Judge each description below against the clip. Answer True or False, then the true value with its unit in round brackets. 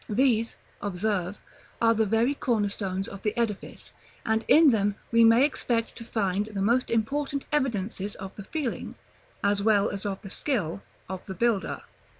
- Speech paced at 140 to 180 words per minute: True (165 wpm)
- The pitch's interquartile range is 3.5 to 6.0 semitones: False (2.9 semitones)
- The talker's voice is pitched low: False (215 Hz)